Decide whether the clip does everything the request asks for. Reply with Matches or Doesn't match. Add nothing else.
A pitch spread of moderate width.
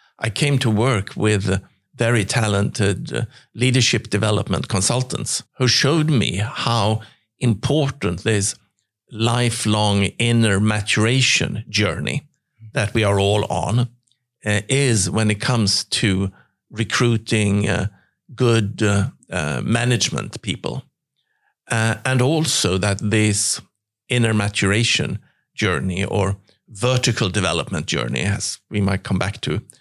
Matches